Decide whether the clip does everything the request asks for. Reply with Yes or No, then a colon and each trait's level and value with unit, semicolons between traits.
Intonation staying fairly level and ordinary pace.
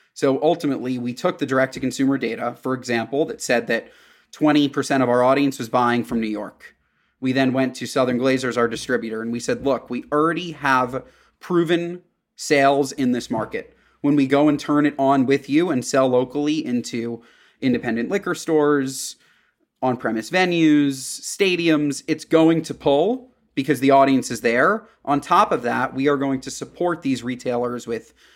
No: average, 3.4 semitones; average, 180 wpm